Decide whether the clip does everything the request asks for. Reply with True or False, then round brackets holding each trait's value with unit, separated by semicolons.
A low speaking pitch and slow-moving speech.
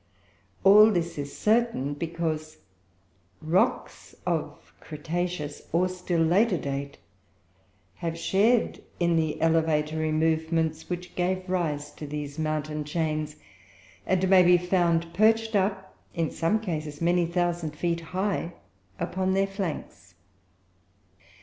False (170 Hz; 115 wpm)